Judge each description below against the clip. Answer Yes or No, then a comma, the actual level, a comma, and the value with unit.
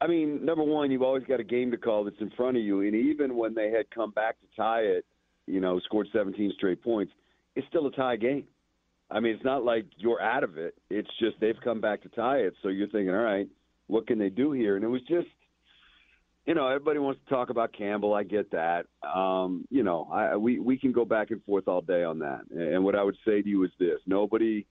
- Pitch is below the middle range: Yes, low, 110 Hz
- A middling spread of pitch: Yes, average, 4.0 semitones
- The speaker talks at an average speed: No, fast, 255 wpm